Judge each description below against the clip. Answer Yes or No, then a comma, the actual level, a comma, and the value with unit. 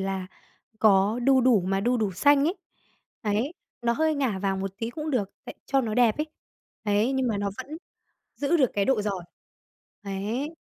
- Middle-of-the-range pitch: No, high, 225 Hz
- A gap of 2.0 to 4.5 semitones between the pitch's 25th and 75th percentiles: No, average, 5.1 semitones